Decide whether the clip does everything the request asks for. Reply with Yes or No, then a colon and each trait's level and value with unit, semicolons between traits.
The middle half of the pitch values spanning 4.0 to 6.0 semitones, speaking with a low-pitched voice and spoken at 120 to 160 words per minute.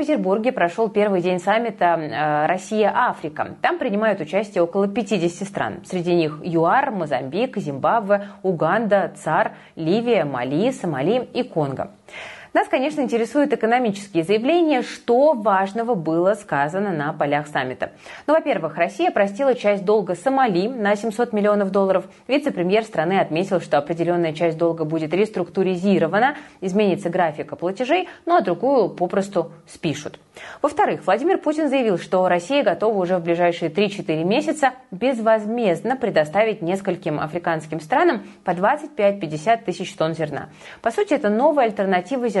No: wide, 5.5 semitones; high, 200 Hz; average, 130 wpm